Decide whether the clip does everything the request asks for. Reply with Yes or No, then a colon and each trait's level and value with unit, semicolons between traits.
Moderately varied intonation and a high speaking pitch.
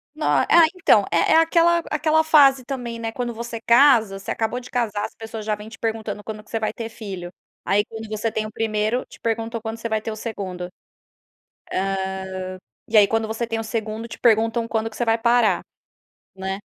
No: narrow, 1.7 semitones; high, 225 Hz